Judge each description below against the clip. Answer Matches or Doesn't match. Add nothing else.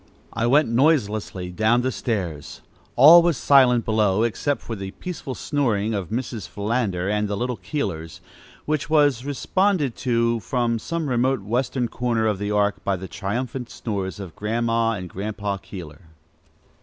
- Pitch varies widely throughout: Doesn't match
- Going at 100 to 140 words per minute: Doesn't match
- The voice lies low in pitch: Matches